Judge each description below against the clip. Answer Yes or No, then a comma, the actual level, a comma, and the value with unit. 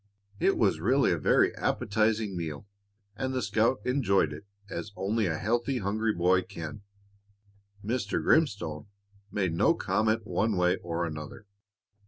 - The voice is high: No, low, 100 Hz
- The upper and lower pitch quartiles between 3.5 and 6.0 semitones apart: Yes, average, 4.5 semitones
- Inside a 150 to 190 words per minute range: No, average, 140 wpm